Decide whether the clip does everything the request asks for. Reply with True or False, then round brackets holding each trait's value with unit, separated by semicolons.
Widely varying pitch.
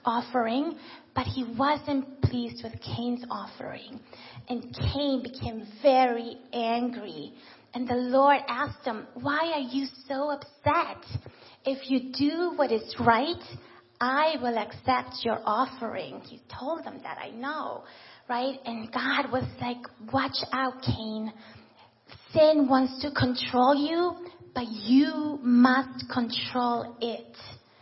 False (3.2 semitones)